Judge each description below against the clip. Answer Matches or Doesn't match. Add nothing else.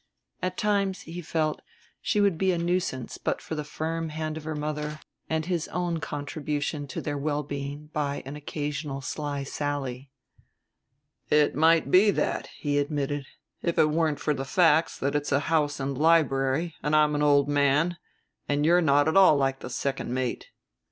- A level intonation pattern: Matches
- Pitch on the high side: Doesn't match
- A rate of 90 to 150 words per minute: Doesn't match